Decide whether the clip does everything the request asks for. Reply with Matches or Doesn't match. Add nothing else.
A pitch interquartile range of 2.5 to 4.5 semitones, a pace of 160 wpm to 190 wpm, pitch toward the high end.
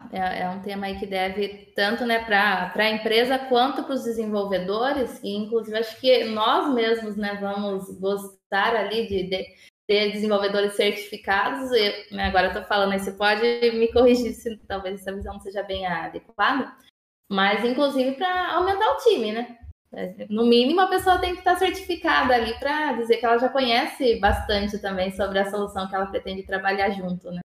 Matches